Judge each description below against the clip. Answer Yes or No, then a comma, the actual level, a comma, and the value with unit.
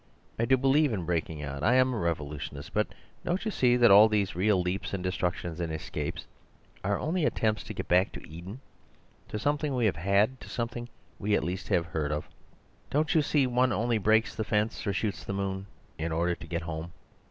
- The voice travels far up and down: Yes, wide, 6.1 semitones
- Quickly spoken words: Yes, fast, 210 wpm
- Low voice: Yes, low, 100 Hz